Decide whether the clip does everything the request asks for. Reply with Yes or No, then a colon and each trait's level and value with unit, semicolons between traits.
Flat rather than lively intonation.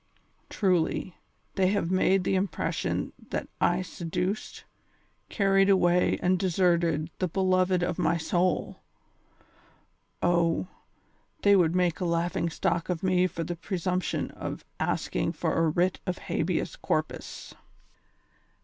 Yes: narrow, 1.6 semitones